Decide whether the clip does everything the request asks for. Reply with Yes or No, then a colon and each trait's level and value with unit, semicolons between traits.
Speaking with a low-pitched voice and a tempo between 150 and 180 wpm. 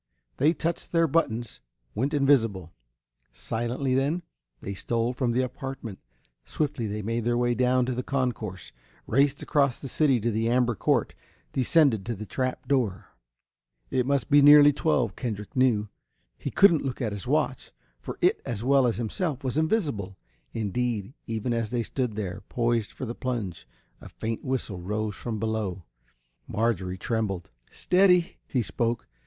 Yes: low, 120 Hz; average, 160 wpm